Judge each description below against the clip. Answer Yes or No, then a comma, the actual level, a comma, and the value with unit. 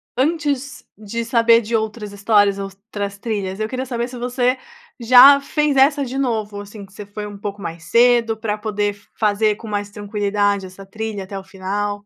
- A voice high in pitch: Yes, high, 215 Hz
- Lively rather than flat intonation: No, average, 2.9 semitones